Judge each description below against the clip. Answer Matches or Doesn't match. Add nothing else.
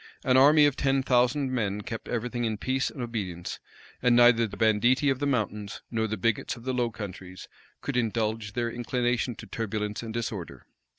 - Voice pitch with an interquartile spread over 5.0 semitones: Doesn't match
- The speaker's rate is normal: Matches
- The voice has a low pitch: Matches